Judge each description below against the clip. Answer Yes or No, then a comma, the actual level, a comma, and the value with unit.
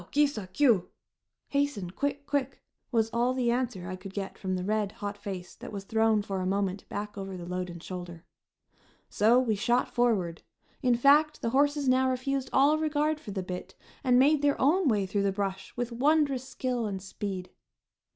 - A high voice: Yes, high, 225 Hz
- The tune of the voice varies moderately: No, wide, 5.8 semitones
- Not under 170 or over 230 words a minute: Yes, average, 190 wpm